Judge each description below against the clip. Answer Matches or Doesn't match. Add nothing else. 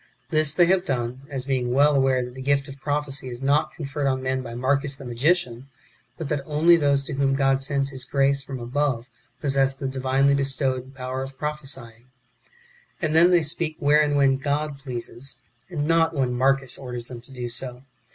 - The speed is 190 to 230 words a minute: Matches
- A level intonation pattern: Matches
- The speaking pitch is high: Doesn't match